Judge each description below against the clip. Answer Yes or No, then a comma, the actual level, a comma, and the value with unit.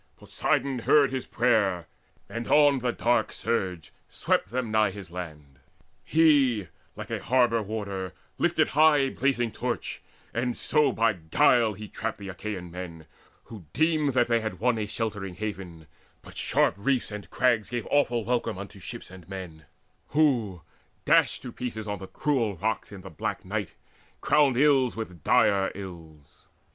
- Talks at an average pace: Yes, average, 160 wpm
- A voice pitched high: No, low, 110 Hz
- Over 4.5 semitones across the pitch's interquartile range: Yes, average, 4.9 semitones